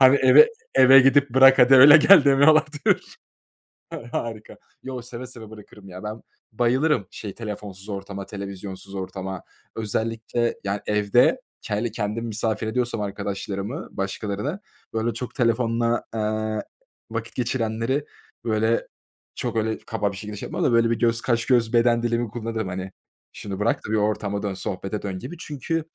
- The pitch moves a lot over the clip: No, average, 3.1 semitones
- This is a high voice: No, low, 115 Hz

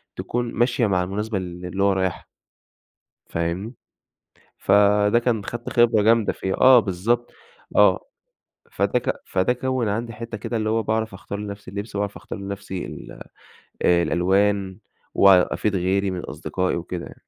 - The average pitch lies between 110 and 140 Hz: No, low, 100 Hz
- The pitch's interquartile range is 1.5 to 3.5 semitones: Yes, average, 3.2 semitones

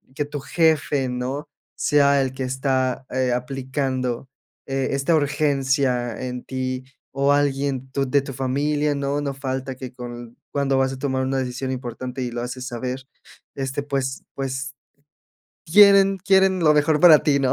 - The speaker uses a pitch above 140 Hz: No, low, 135 Hz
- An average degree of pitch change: No, narrow, 1.8 semitones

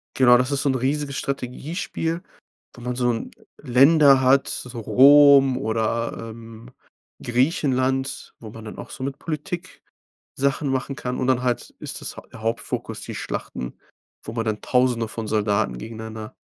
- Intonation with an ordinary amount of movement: Yes, average, 3.3 semitones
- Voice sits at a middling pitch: No, low, 125 Hz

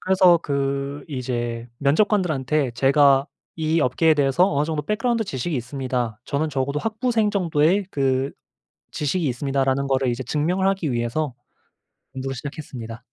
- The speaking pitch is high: No, medium, 140 Hz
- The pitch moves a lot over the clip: No, average, 3.7 semitones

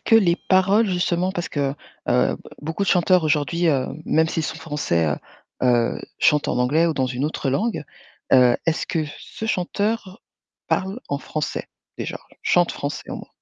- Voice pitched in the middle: Yes, medium, 160 Hz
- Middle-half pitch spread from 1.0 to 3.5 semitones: No, average, 4.8 semitones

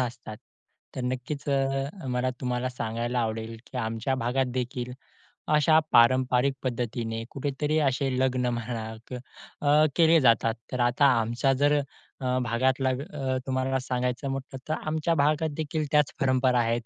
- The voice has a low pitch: Yes, low, 130 Hz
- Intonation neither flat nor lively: No, narrow, 2.3 semitones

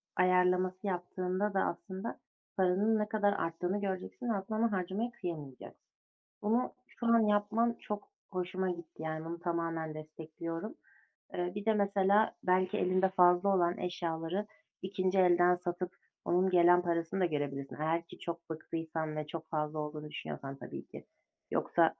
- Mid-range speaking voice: Yes, medium, 180 Hz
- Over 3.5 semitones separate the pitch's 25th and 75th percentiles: No, average, 3.0 semitones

